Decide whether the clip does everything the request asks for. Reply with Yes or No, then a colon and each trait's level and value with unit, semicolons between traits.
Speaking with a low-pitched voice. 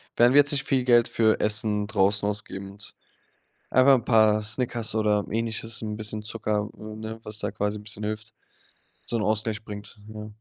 Yes: low, 110 Hz